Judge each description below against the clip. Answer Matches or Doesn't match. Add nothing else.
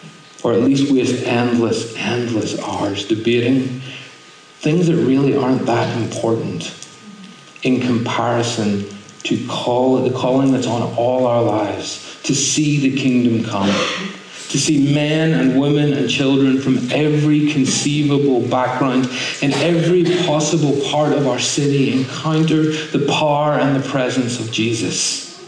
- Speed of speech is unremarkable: Doesn't match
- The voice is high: Doesn't match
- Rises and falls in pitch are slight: Doesn't match